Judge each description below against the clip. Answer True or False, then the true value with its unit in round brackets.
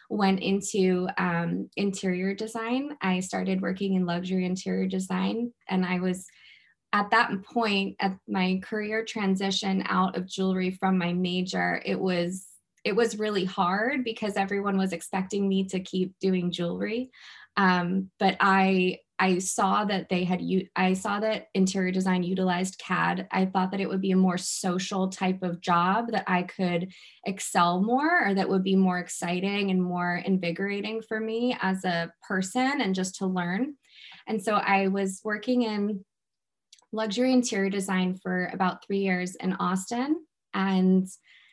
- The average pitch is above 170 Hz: True (190 Hz)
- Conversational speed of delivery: True (155 wpm)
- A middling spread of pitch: False (1.7 semitones)